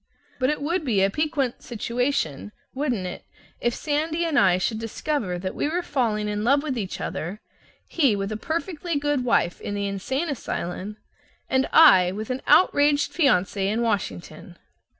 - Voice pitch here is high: Yes, high, 240 Hz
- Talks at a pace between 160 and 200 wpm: Yes, average, 170 wpm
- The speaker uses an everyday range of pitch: No, wide, 6.6 semitones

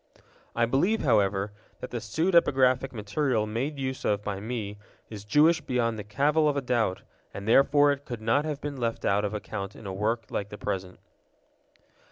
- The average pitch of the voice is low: Yes, low, 115 Hz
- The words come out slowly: No, average, 185 wpm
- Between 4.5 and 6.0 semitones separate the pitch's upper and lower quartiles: Yes, average, 5.1 semitones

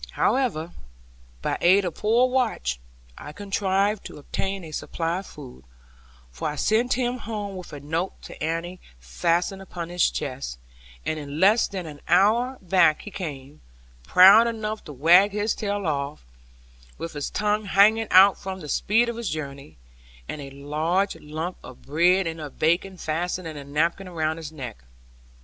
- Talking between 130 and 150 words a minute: No, average, 165 wpm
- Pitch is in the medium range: Yes, medium, 175 Hz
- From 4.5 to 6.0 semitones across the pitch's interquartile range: Yes, average, 5.0 semitones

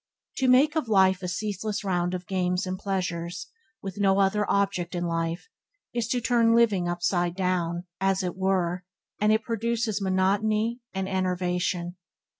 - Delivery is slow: No, average, 155 wpm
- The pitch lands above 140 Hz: Yes, high, 190 Hz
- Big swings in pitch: No, average, 3.1 semitones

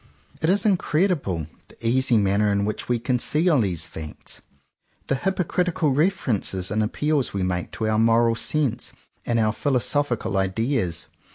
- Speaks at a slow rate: No, average, 155 wpm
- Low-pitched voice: Yes, low, 120 Hz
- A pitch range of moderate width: No, wide, 6.4 semitones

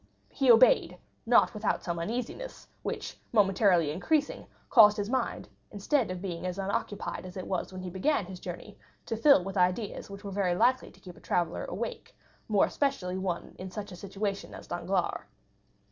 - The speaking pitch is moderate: No, high, 195 Hz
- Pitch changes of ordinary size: Yes, average, 3.7 semitones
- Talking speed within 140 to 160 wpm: No, average, 175 wpm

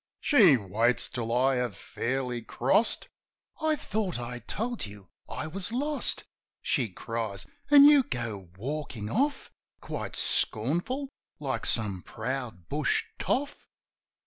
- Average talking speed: No, slow, 120 wpm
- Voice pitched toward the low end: Yes, low, 130 Hz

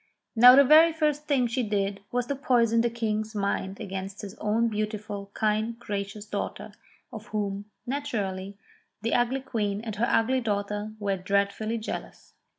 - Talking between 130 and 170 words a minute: Yes, average, 160 wpm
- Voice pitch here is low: No, high, 215 Hz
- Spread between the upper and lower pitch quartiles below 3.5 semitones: Yes, average, 3.1 semitones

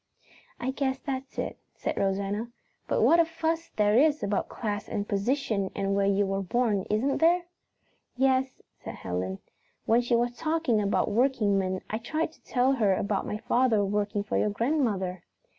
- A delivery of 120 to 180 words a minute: Yes, average, 170 wpm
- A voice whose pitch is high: Yes, high, 220 Hz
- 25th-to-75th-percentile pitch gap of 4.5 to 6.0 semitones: Yes, average, 4.9 semitones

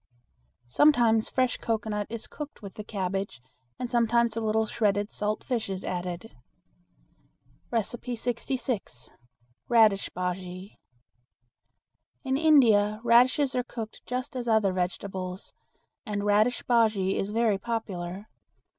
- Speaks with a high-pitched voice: Yes, high, 220 Hz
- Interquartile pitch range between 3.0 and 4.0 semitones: Yes, average, 3.4 semitones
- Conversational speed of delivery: No, slow, 110 wpm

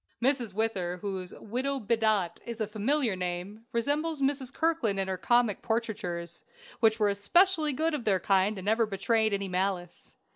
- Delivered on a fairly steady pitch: No, average, 4.2 semitones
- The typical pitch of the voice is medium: No, high, 220 Hz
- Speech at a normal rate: Yes, average, 160 wpm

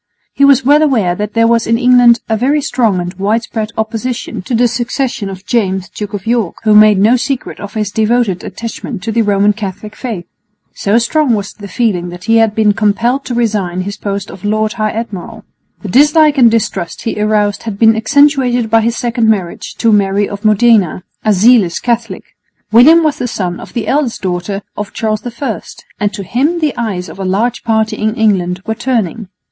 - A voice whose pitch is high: Yes, high, 220 Hz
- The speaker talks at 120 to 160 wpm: No, average, 200 wpm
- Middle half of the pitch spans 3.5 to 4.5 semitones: No, average, 3.0 semitones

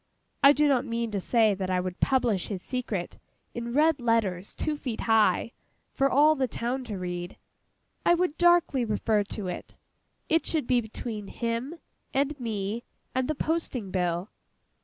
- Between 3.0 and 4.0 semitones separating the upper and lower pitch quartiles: No, average, 5.2 semitones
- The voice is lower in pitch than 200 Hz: No, high, 235 Hz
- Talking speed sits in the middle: Yes, average, 165 wpm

